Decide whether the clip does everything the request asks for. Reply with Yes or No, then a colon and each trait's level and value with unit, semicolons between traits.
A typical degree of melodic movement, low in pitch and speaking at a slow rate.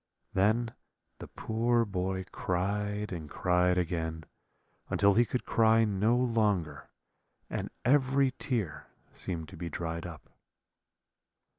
Yes: average, 4.5 semitones; low, 100 Hz; slow, 115 wpm